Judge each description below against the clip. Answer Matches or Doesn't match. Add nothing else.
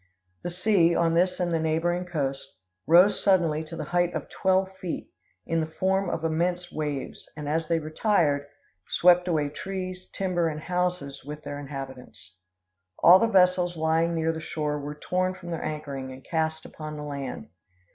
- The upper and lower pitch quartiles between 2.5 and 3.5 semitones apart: Matches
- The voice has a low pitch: Doesn't match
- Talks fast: Doesn't match